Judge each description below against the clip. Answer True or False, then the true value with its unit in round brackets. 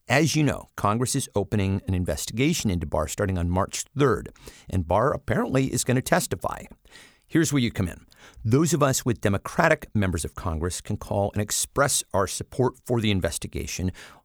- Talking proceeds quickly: False (180 wpm)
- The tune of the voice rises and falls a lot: True (6.1 semitones)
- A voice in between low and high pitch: False (105 Hz)